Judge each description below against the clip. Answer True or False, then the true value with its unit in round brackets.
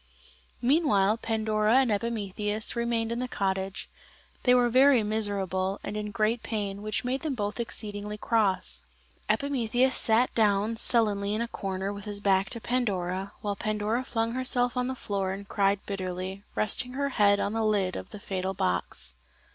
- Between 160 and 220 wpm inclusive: True (165 wpm)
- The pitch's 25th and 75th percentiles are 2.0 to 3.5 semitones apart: True (3.0 semitones)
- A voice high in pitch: True (210 Hz)